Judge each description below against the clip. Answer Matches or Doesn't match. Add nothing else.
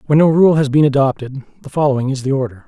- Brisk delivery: Matches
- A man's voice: Matches